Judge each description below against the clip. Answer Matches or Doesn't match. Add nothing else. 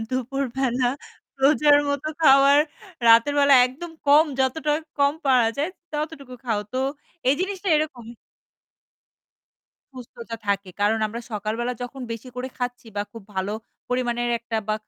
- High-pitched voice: Matches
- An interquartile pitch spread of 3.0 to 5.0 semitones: Matches